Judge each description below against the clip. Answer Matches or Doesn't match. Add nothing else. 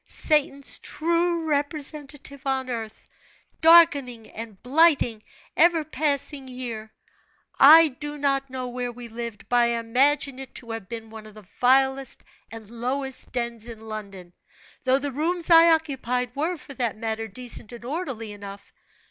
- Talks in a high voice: Matches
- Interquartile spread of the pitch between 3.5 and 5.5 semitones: Matches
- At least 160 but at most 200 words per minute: Doesn't match